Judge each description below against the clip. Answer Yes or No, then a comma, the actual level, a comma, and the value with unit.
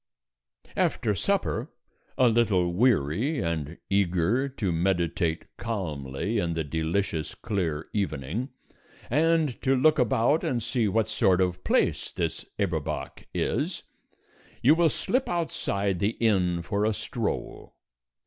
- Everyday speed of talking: No, slow, 120 wpm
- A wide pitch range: Yes, wide, 6.2 semitones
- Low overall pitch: Yes, low, 100 Hz